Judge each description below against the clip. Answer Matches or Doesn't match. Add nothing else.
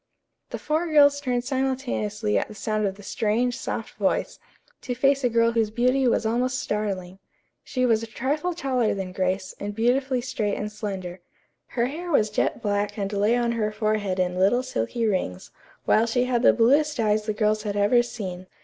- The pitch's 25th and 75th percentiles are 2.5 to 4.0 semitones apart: Matches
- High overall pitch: Matches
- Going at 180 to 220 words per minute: Matches